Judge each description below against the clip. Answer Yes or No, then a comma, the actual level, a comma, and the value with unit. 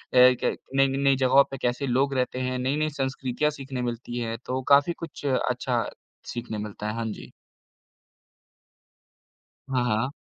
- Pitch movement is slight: Yes, narrow, 2.1 semitones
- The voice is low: Yes, low, 130 Hz